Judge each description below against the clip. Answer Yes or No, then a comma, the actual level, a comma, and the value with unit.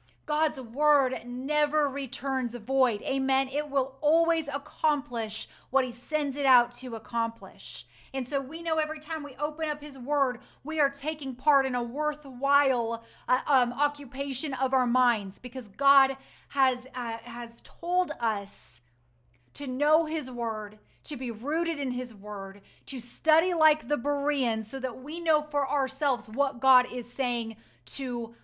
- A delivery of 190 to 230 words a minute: No, average, 160 wpm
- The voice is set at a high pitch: Yes, very high, 270 Hz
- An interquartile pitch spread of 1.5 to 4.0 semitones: Yes, average, 3.3 semitones